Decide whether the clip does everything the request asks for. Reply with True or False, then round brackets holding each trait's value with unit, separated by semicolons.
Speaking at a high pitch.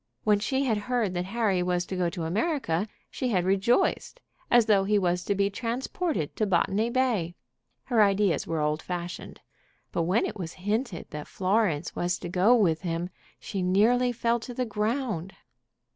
True (200 Hz)